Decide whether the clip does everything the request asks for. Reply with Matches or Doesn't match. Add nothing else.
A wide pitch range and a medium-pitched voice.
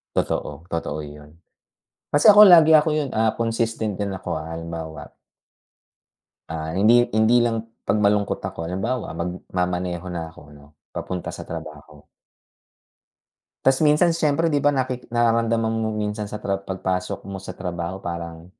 Doesn't match